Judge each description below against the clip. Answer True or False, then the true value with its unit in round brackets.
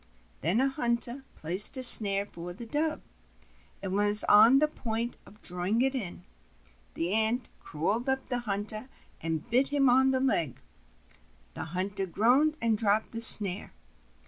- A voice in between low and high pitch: False (220 Hz)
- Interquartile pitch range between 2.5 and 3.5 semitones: False (4.7 semitones)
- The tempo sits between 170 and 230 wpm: False (160 wpm)